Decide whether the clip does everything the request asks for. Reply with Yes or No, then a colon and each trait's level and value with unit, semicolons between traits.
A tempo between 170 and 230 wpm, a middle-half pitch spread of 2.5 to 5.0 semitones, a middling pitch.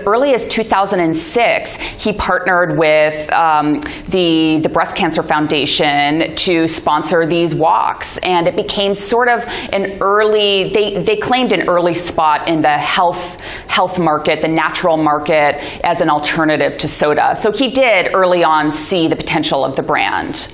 No: average, 155 wpm; average, 3.9 semitones; medium, 170 Hz